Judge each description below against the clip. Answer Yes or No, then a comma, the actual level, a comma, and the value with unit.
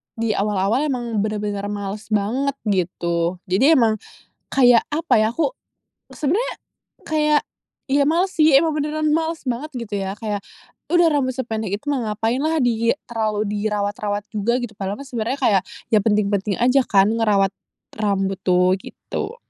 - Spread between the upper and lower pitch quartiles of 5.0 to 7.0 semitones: Yes, wide, 5.5 semitones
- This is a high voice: Yes, high, 225 Hz